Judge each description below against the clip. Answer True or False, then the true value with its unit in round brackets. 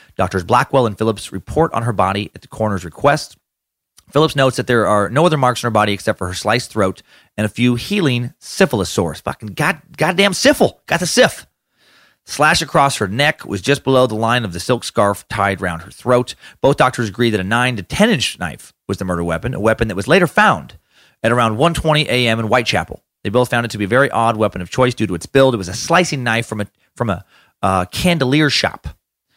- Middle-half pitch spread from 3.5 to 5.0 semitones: True (4.6 semitones)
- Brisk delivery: True (230 wpm)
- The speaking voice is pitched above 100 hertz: True (120 Hz)